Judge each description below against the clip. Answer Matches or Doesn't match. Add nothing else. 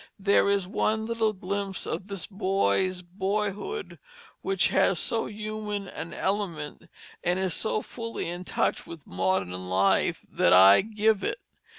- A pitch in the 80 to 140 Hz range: Doesn't match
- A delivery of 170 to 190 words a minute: Doesn't match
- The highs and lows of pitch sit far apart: Doesn't match